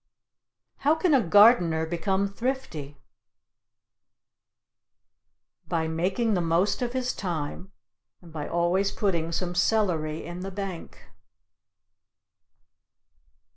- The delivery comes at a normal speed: No, slow, 95 wpm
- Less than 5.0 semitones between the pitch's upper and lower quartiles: Yes, average, 4.0 semitones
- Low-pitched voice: No, medium, 180 Hz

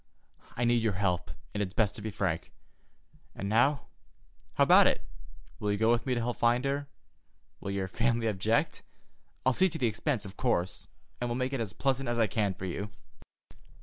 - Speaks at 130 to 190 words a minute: No, average, 200 wpm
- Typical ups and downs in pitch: Yes, average, 3.5 semitones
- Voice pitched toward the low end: Yes, low, 115 Hz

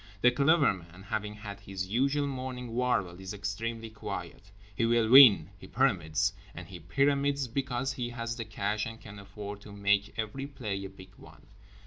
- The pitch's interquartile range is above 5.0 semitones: No, average, 4.2 semitones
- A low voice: Yes, low, 110 Hz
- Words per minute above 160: Yes, average, 170 wpm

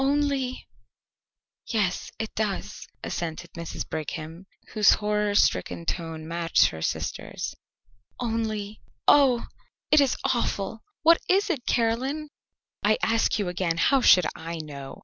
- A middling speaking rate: No, slow, 130 wpm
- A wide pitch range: Yes, wide, 6.9 semitones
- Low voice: No, high, 210 Hz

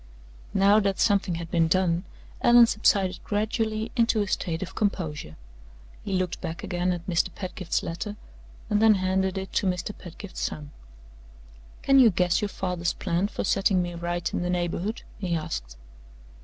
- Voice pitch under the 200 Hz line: Yes, medium, 185 Hz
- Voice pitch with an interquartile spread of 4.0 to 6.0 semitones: No, average, 3.0 semitones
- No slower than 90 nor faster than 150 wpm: No, average, 165 wpm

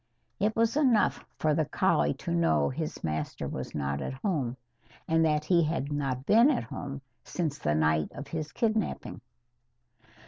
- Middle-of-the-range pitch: Yes, medium, 145 Hz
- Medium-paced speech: Yes, average, 165 wpm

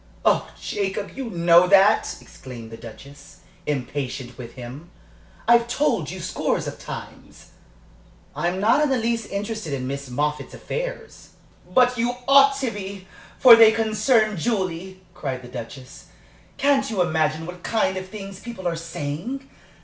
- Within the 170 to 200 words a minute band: No, average, 150 wpm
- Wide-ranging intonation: Yes, wide, 7.5 semitones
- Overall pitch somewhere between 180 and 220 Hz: Yes, high, 190 Hz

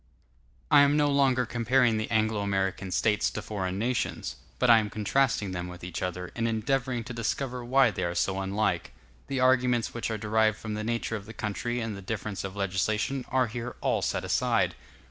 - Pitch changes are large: No, average, 3.8 semitones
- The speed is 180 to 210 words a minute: Yes, average, 200 wpm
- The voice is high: No, low, 110 Hz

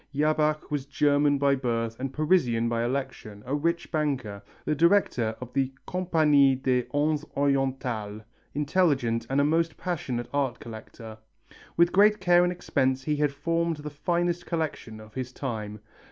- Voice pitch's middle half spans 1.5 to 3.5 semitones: No, average, 4.2 semitones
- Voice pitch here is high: No, medium, 140 Hz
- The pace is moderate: Yes, average, 155 wpm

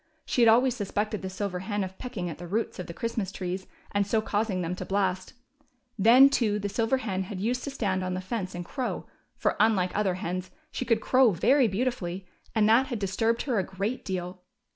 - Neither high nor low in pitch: No, high, 205 Hz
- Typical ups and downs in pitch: Yes, average, 3.7 semitones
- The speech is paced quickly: Yes, fast, 215 wpm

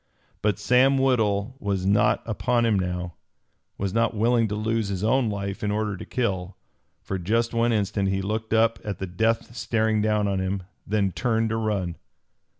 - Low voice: Yes, low, 105 Hz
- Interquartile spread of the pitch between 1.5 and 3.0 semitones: Yes, narrow, 2.5 semitones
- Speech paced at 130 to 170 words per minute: No, average, 180 wpm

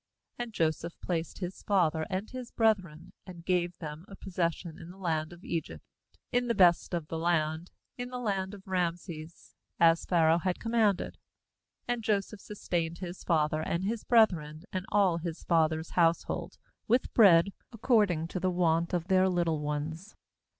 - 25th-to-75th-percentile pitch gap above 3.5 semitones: No, average, 3.2 semitones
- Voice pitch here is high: No, medium, 175 Hz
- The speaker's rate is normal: Yes, average, 170 wpm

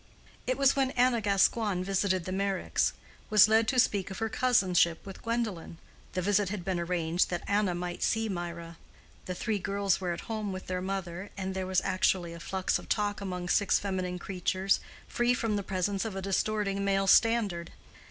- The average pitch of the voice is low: No, high, 195 Hz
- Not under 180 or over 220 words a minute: Yes, average, 190 wpm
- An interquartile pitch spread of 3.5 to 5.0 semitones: No, narrow, 2.5 semitones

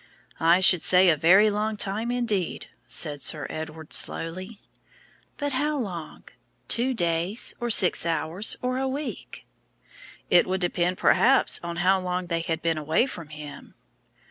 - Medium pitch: Yes, medium, 180 Hz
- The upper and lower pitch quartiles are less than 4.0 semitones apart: No, average, 4.9 semitones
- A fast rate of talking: No, average, 150 wpm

